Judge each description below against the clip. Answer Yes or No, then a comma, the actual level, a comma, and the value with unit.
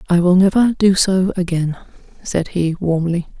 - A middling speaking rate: Yes, average, 160 wpm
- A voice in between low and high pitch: Yes, medium, 180 Hz